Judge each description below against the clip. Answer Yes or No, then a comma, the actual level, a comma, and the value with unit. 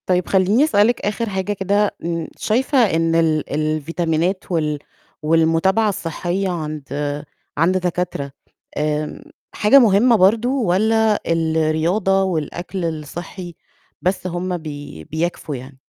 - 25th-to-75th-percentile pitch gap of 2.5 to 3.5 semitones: No, average, 4.0 semitones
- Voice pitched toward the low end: No, medium, 175 Hz